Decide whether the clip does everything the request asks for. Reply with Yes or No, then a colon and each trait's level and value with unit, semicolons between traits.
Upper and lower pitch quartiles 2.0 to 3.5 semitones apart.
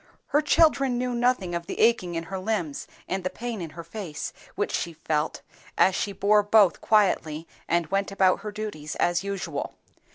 No: average, 4.2 semitones